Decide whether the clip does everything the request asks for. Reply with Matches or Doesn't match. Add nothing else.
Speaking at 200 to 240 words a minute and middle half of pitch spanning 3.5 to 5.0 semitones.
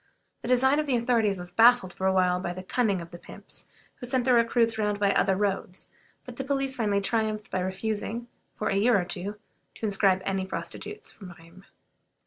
Matches